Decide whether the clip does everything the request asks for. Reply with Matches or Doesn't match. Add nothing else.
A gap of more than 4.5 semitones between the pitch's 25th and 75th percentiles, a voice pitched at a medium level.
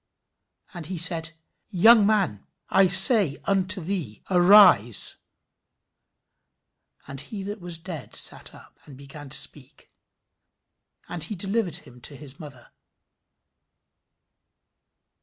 Matches